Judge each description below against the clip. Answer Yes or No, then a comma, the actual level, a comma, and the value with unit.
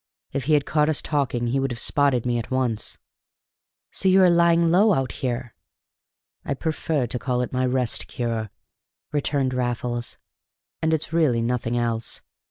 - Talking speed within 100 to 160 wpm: No, average, 170 wpm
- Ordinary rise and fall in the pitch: Yes, average, 4.0 semitones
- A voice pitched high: No, low, 130 Hz